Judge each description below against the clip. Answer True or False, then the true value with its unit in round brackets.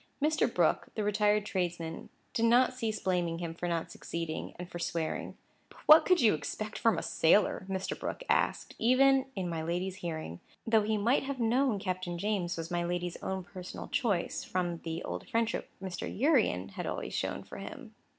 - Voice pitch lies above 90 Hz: True (190 Hz)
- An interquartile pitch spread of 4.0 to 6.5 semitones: True (4.8 semitones)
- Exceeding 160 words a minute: True (185 wpm)